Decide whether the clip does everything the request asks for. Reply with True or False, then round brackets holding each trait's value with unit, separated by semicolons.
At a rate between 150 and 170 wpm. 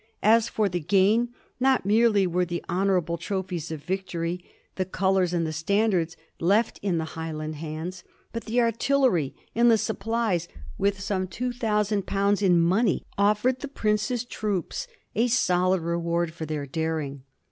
True (160 wpm)